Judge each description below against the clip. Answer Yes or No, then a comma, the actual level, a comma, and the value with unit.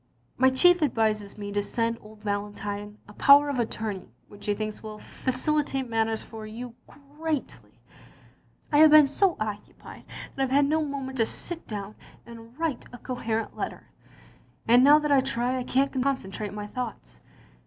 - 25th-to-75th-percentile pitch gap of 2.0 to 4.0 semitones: No, average, 4.7 semitones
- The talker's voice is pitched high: Yes, high, 235 Hz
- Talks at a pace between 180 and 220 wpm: No, average, 170 wpm